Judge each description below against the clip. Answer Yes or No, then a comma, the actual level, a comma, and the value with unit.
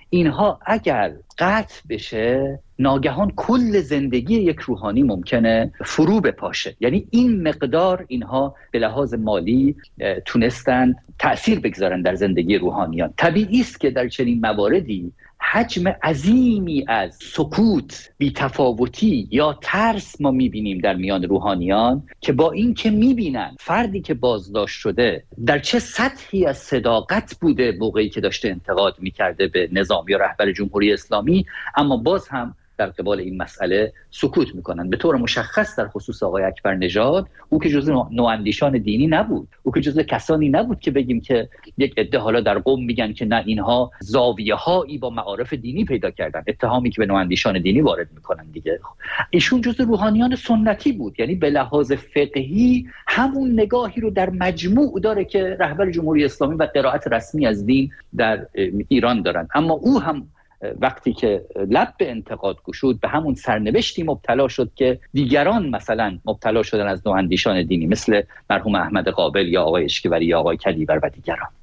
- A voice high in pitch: No, medium, 140 Hz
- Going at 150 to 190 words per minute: Yes, fast, 155 wpm